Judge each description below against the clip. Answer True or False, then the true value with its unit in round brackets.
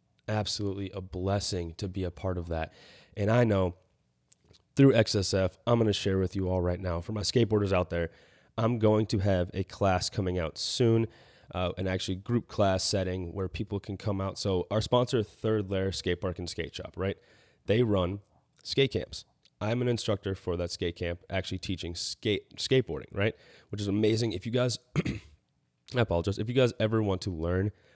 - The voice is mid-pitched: False (95 Hz)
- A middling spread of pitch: True (3.2 semitones)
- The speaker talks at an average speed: True (190 wpm)